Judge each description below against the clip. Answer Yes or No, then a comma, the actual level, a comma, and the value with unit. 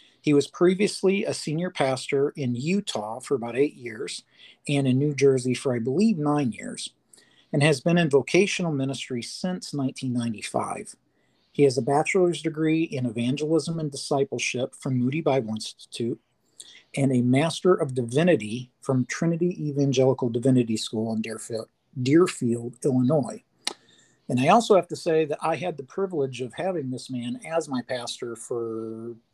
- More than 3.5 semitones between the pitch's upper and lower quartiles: Yes, average, 4.3 semitones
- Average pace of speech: Yes, average, 155 wpm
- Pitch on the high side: No, low, 135 Hz